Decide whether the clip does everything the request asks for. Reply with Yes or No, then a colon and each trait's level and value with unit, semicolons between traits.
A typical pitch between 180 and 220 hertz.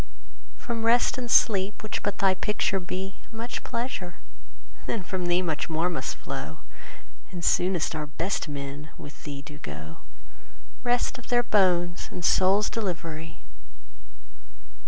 Yes: medium, 185 Hz